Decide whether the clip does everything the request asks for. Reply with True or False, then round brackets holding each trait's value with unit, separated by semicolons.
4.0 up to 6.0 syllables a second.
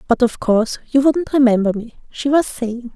True (5.1 syllables/s)